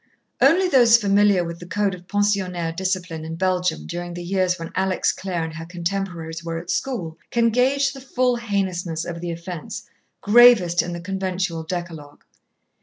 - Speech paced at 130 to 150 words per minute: No, average, 170 wpm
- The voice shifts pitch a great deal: No, average, 3.4 semitones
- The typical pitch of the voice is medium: Yes, medium, 180 Hz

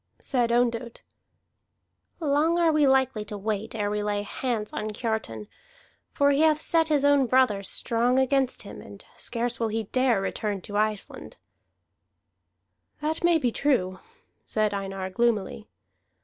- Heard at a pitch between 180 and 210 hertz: No, high, 235 Hz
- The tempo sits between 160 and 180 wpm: No, average, 145 wpm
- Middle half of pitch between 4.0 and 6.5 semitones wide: Yes, average, 4.7 semitones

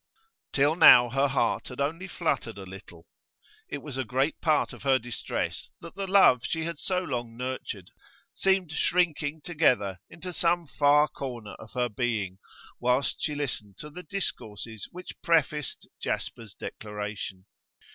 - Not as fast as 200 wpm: Yes, average, 150 wpm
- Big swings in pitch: Yes, wide, 6.1 semitones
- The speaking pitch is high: No, low, 135 Hz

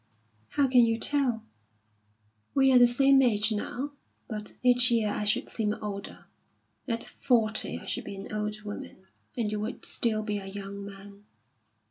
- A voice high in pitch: Yes, high, 215 Hz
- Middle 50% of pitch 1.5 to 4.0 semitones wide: Yes, average, 2.8 semitones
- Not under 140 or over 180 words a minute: Yes, average, 165 wpm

